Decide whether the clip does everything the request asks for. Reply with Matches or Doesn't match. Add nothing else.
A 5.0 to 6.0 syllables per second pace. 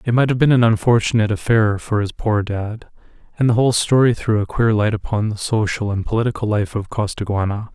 Matches